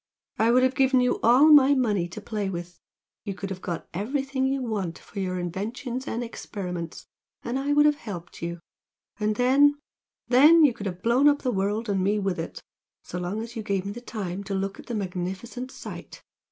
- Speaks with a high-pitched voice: Yes, high, 215 Hz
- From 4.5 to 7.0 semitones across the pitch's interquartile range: Yes, average, 5.3 semitones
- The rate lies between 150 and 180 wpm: No, fast, 205 wpm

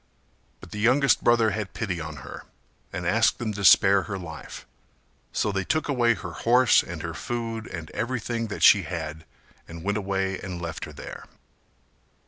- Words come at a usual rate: Yes, average, 175 wpm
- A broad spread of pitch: No, average, 5.0 semitones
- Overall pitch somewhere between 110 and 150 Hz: No, low, 100 Hz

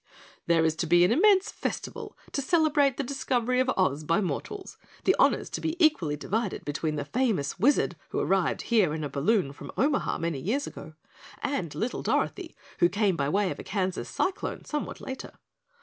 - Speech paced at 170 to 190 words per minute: Yes, average, 185 wpm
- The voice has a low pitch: No, high, 205 Hz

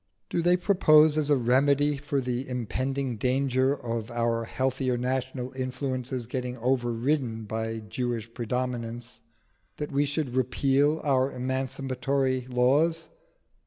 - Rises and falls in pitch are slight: Yes, narrow, 2.3 semitones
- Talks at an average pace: No, slow, 120 wpm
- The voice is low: Yes, low, 130 Hz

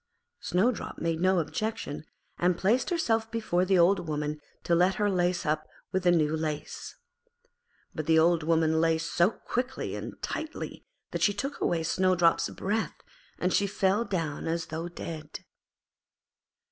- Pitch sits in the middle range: Yes, medium, 175 Hz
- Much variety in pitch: No, average, 3.8 semitones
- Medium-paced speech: Yes, average, 150 wpm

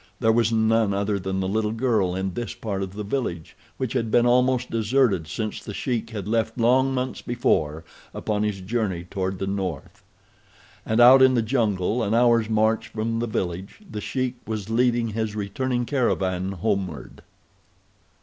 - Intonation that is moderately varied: Yes, average, 3.6 semitones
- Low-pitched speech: Yes, low, 110 Hz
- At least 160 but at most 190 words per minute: Yes, average, 170 wpm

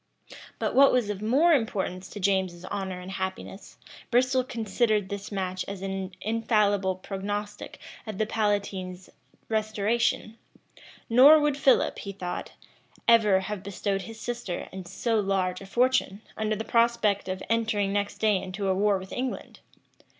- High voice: Yes, high, 205 Hz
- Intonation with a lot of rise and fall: No, average, 3.0 semitones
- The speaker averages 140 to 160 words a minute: Yes, average, 150 wpm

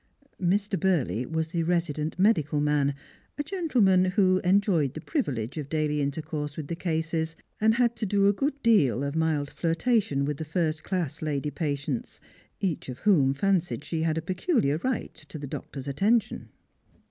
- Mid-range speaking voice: Yes, medium, 160 Hz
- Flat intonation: No, average, 5.0 semitones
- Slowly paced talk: No, average, 170 wpm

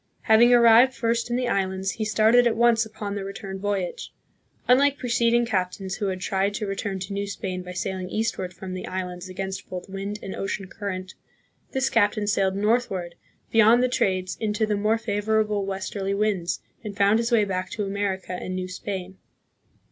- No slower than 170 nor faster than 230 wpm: Yes, average, 180 wpm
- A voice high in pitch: Yes, high, 200 Hz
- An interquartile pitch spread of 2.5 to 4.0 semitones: Yes, average, 2.8 semitones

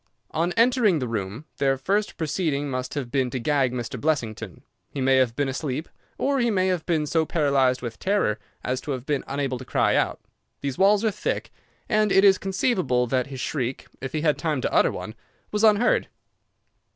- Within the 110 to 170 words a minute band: No, average, 200 wpm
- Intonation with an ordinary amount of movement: No, wide, 6.6 semitones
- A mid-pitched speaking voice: Yes, medium, 145 Hz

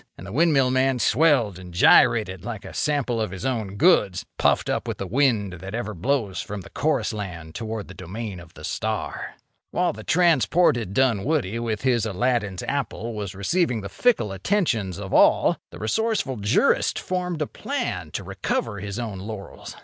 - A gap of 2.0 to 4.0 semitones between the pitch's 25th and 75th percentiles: No, wide, 5.4 semitones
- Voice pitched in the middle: No, low, 110 Hz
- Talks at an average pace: Yes, average, 175 wpm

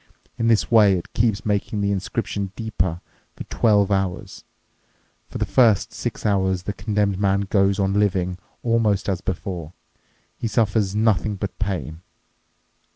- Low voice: Yes, low, 100 Hz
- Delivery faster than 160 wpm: No, average, 145 wpm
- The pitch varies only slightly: Yes, narrow, 2.1 semitones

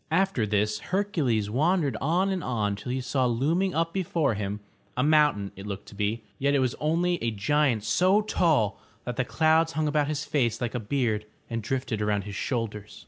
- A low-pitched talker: Yes, low, 130 Hz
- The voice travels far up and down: Yes, wide, 6.8 semitones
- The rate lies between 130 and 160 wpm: No, average, 200 wpm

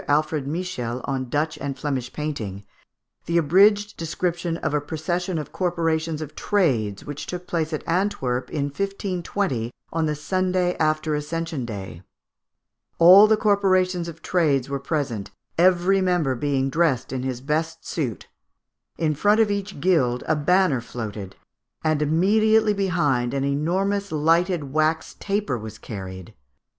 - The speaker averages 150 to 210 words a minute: No, average, 140 wpm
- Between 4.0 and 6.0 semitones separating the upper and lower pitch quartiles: Yes, average, 5.0 semitones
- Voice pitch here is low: No, medium, 155 Hz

